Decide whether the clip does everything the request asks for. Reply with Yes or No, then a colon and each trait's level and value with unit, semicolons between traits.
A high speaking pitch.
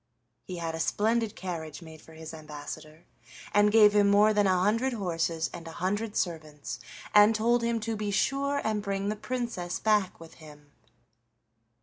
Yes: high, 200 Hz